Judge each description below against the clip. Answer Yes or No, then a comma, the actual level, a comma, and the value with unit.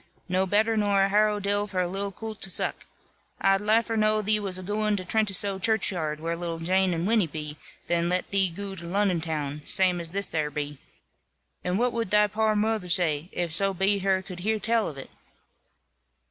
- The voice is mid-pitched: No, high, 195 Hz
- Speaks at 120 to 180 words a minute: No, fast, 205 wpm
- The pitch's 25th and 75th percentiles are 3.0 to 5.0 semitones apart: Yes, average, 3.3 semitones